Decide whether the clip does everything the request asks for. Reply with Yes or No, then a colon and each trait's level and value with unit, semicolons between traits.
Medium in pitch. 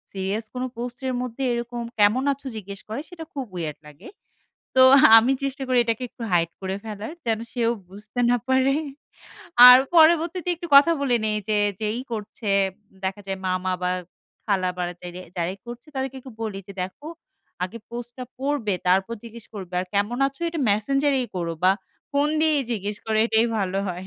No: high, 225 Hz